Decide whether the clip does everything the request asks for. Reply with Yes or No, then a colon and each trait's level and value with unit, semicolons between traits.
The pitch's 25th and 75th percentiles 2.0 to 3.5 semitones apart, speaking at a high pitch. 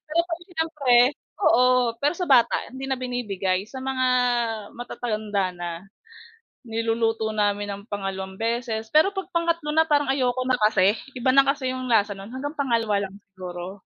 No: average, 4.7 semitones; high, 245 Hz